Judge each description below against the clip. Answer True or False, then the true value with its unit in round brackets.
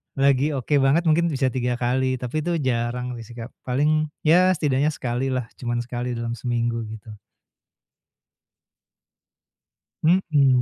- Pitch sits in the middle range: False (130 Hz)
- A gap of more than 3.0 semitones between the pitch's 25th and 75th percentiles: True (3.7 semitones)